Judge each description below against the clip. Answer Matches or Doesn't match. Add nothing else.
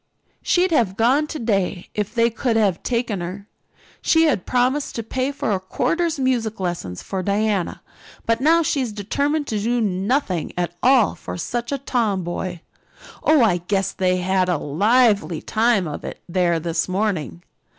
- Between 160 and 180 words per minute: Matches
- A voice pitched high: Matches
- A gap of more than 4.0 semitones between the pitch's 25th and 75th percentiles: Matches